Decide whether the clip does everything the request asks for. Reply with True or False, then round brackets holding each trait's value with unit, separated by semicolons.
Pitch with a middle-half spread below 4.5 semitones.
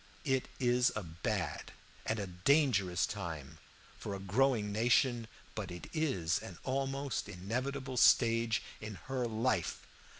False (5.3 semitones)